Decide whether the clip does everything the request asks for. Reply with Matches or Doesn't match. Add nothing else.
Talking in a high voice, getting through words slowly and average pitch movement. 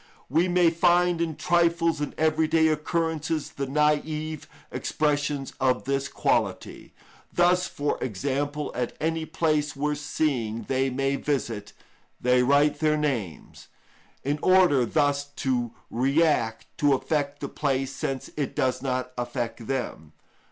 Doesn't match